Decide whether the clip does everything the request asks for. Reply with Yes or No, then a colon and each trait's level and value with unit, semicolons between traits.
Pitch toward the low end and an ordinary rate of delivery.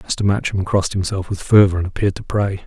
No: very low, 95 Hz; fast, 225 wpm